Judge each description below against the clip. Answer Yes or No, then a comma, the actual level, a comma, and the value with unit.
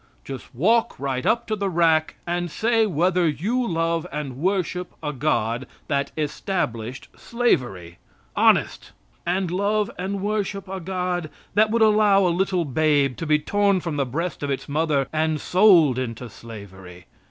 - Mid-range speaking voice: Yes, medium, 165 Hz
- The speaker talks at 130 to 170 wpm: Yes, average, 155 wpm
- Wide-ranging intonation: Yes, wide, 5.9 semitones